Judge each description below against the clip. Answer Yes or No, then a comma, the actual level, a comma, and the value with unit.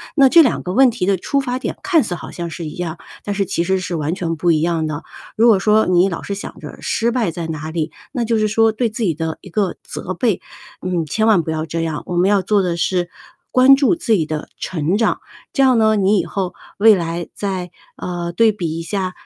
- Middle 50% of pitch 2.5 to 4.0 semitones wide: No, average, 4.6 semitones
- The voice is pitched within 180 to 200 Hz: Yes, medium, 185 Hz